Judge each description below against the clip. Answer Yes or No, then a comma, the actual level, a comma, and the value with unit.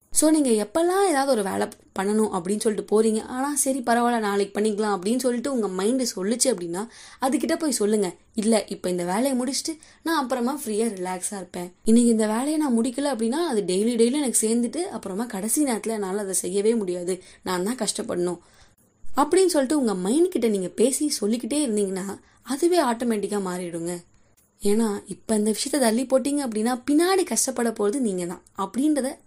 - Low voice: No, high, 225 Hz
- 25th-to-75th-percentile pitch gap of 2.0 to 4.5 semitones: No, average, 5.0 semitones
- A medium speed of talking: No, fast, 160 wpm